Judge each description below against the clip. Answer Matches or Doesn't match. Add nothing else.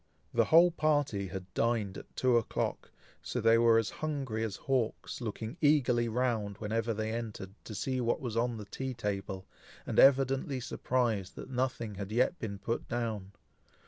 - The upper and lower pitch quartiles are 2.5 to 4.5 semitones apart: Matches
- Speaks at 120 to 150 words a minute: Doesn't match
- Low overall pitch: Matches